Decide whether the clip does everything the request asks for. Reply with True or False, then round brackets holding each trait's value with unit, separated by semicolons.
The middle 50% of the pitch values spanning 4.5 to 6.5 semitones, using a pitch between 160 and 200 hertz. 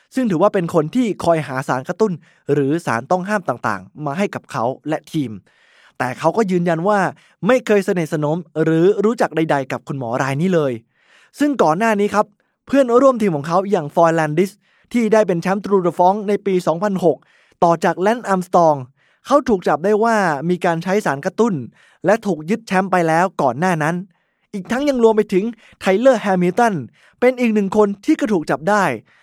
True (4.8 semitones; 185 Hz)